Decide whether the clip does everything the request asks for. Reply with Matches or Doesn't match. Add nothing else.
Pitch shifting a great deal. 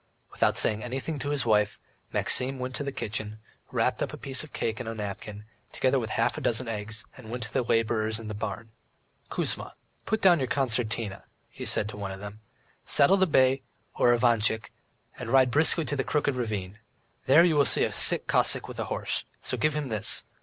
Doesn't match